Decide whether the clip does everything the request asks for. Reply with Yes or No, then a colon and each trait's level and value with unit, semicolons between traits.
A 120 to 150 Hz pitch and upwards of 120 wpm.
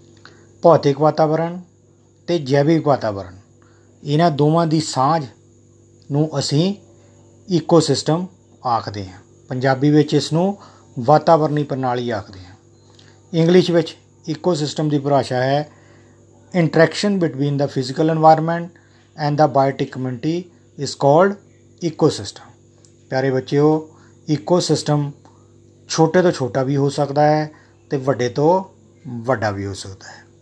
No: medium, 140 Hz; average, 115 wpm